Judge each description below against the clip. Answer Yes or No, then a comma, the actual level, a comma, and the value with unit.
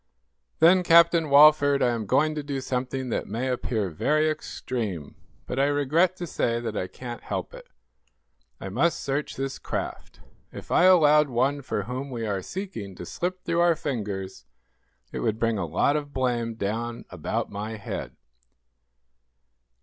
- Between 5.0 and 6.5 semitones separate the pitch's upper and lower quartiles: Yes, average, 5.3 semitones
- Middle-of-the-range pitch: No, low, 130 Hz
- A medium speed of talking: Yes, average, 165 wpm